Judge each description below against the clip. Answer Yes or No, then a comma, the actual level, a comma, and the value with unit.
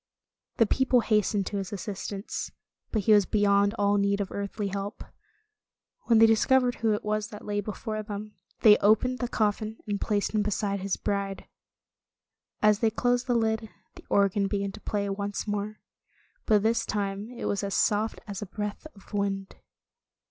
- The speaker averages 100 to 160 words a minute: No, average, 175 wpm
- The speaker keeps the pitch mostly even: Yes, narrow, 1.5 semitones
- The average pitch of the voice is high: Yes, high, 205 Hz